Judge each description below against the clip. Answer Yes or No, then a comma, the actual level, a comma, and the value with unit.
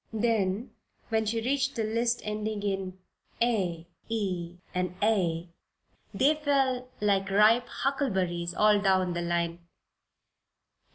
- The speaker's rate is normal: No, slow, 115 wpm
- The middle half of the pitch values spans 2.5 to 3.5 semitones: No, average, 4.2 semitones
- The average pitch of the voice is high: Yes, high, 210 Hz